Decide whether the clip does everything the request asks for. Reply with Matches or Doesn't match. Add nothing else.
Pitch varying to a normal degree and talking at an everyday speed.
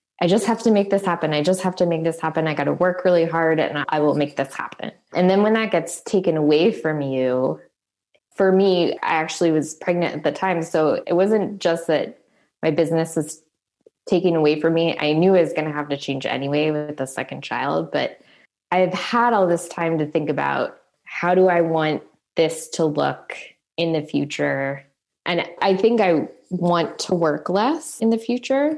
Doesn't match